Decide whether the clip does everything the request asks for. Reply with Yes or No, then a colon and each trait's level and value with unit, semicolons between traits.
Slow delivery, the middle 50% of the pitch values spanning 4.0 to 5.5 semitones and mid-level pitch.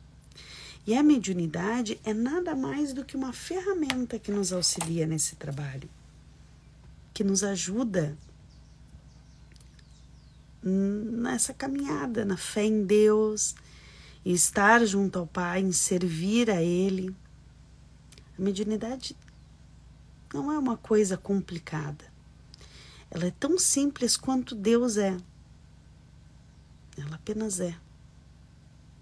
No: slow, 105 wpm; average, 5.1 semitones; high, 205 Hz